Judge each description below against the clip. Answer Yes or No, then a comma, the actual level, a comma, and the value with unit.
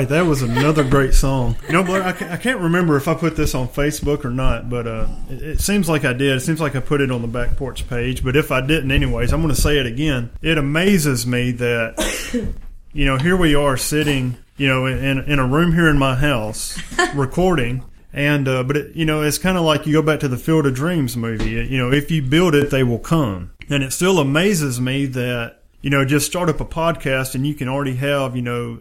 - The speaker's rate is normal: No, fast, 250 wpm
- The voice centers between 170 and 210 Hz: No, medium, 140 Hz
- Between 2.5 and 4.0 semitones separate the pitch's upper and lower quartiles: Yes, average, 3.4 semitones